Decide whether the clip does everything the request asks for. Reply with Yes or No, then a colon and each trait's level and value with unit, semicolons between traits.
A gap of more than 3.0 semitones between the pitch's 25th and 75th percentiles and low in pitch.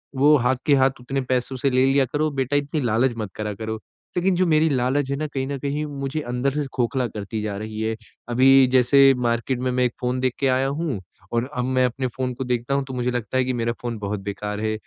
No: average, 2.7 semitones; low, 130 Hz